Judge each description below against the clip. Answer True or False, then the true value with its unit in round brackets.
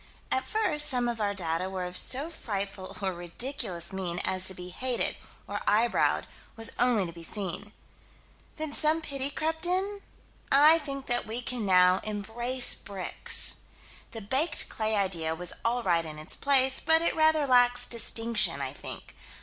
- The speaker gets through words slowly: False (165 wpm)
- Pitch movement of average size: False (6.6 semitones)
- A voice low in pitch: False (230 Hz)